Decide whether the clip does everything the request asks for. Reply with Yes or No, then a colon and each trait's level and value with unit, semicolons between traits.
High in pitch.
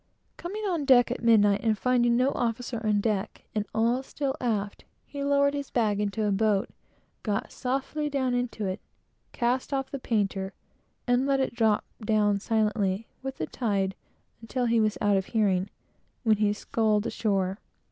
Yes: high, 225 Hz